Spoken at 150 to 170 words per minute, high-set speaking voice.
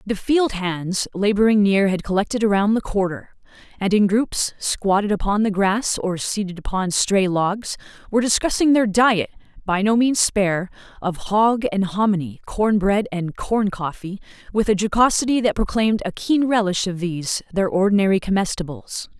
Yes: average, 155 wpm; high, 200 Hz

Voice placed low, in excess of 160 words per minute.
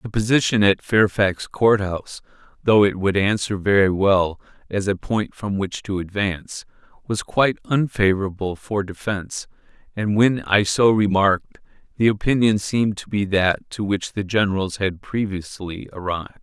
No: low, 100 Hz; average, 155 wpm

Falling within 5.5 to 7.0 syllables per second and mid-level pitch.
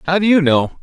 Yes: 6.0 syllables/s; medium, 165 Hz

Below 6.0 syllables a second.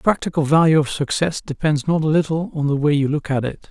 No: 6.1 syllables/s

